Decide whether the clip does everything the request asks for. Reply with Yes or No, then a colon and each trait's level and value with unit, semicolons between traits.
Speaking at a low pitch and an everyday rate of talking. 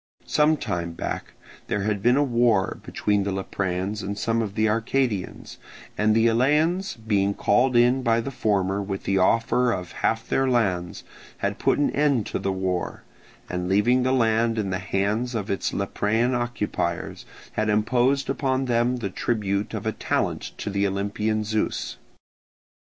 Yes: low, 110 Hz; average, 165 wpm